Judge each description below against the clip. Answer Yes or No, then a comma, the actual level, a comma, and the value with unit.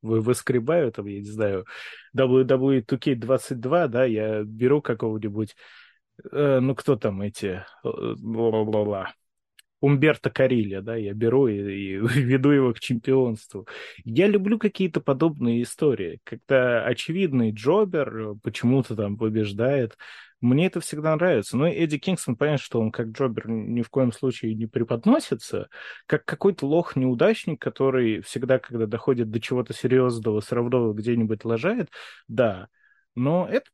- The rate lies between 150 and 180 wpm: No, average, 135 wpm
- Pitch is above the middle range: No, low, 125 Hz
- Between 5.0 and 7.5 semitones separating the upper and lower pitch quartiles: No, average, 3.8 semitones